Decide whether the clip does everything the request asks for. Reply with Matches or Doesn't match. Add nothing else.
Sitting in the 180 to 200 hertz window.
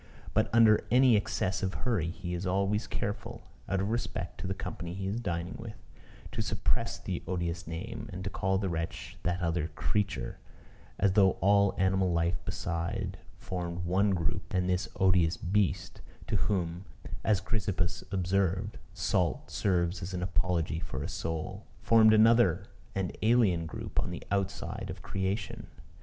Doesn't match